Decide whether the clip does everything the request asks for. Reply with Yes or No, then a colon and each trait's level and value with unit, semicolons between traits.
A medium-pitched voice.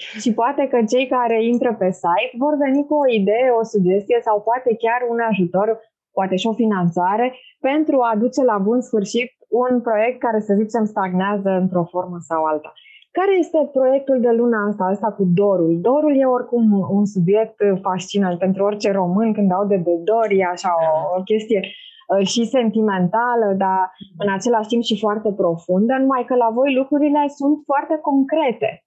No: high, 220 Hz